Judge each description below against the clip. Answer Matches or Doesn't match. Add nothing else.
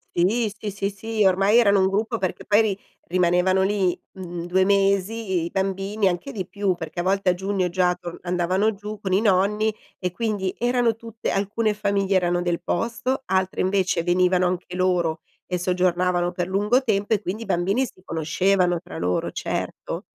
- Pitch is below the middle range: Doesn't match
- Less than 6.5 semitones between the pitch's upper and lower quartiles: Matches